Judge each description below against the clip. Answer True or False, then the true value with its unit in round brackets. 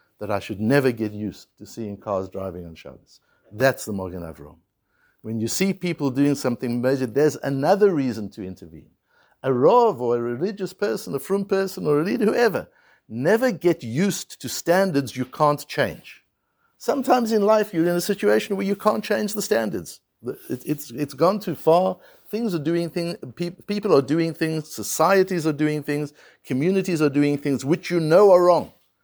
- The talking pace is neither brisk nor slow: True (180 wpm)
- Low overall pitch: False (150 Hz)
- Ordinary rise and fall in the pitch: False (7.8 semitones)